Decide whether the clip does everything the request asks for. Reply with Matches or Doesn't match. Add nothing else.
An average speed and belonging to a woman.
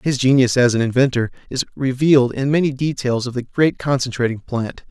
Doesn't match